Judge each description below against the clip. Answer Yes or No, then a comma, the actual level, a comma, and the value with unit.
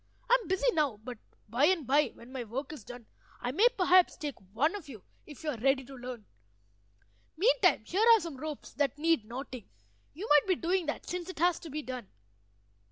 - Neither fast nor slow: No, fast, 210 wpm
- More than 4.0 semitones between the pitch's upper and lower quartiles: Yes, wide, 5.6 semitones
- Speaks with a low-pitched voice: No, very high, 295 Hz